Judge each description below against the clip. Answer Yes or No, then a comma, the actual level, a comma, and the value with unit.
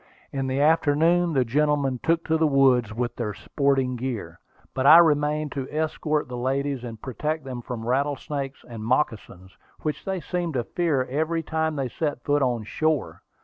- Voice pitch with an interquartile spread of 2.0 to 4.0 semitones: Yes, average, 3.7 semitones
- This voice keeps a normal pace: Yes, average, 175 wpm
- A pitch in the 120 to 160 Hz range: Yes, medium, 140 Hz